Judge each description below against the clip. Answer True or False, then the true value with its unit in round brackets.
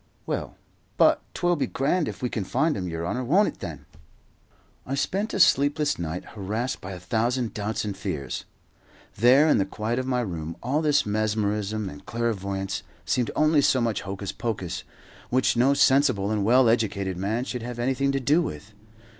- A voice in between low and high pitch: False (115 Hz)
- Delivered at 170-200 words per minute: True (180 wpm)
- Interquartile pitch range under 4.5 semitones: False (5.3 semitones)